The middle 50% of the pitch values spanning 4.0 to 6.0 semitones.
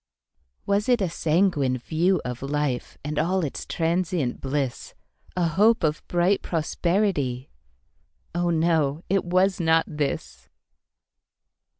Yes: average, 4.3 semitones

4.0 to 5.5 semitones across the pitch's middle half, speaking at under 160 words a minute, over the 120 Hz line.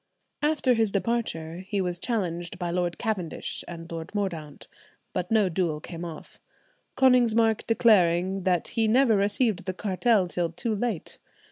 Yes: average, 4.5 semitones; average, 145 wpm; high, 190 Hz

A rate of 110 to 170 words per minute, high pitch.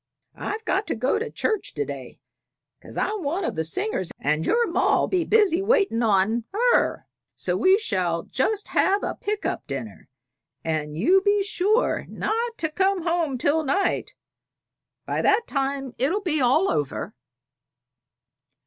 Yes: average, 155 wpm; very high, 360 Hz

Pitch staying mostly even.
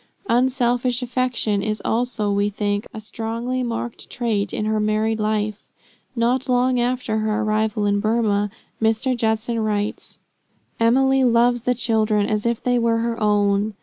Yes: narrow, 2.3 semitones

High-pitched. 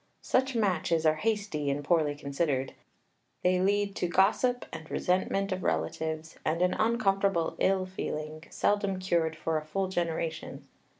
No: medium, 180 Hz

